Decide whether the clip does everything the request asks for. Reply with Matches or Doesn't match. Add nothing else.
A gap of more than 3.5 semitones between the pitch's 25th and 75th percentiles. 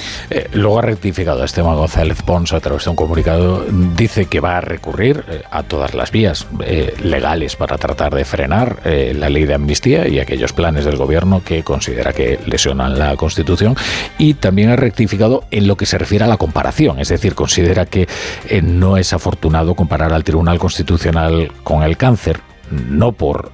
Matches